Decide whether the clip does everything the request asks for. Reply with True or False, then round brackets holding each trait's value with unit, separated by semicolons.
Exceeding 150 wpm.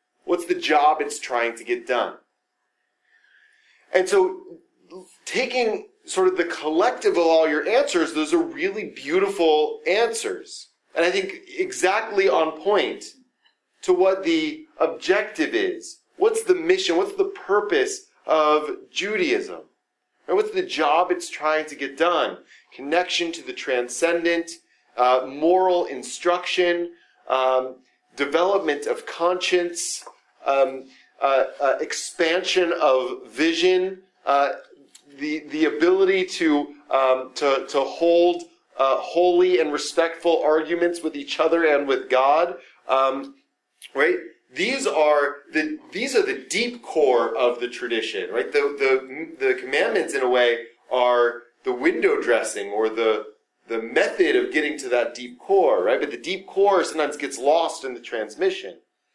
False (135 wpm)